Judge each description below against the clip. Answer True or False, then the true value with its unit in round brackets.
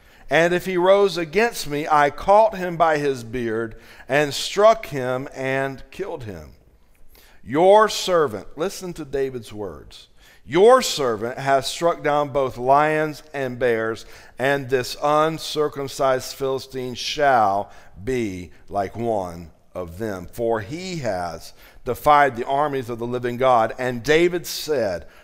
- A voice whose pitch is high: False (135 Hz)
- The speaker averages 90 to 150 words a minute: True (135 wpm)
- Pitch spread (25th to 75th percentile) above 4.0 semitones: True (4.7 semitones)